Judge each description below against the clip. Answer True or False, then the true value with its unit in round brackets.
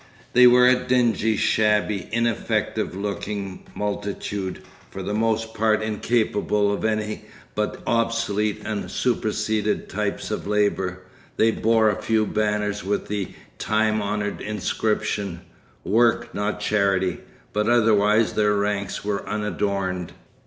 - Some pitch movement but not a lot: False (1.4 semitones)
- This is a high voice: False (105 Hz)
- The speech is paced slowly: True (120 wpm)